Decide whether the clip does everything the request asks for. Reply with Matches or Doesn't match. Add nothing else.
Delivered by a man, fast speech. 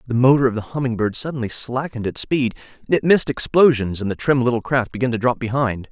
Matches